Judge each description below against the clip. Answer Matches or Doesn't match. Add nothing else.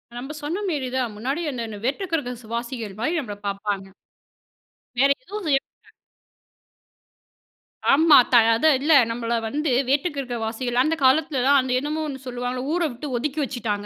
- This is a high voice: Matches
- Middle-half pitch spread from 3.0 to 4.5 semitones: Matches